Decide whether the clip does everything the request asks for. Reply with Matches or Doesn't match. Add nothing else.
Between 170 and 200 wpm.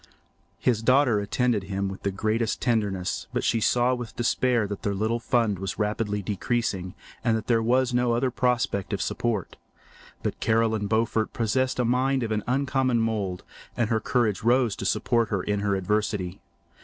Matches